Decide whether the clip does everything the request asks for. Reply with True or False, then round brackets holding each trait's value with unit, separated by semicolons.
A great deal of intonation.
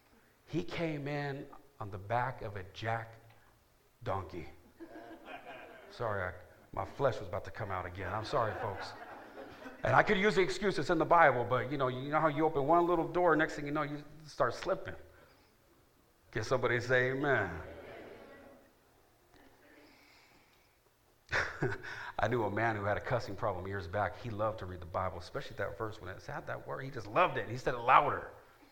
True (6.3 semitones)